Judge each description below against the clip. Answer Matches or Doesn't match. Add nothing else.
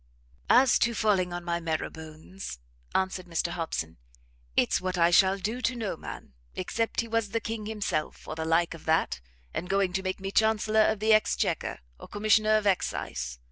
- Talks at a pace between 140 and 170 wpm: Doesn't match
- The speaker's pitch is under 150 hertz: Doesn't match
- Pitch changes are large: Doesn't match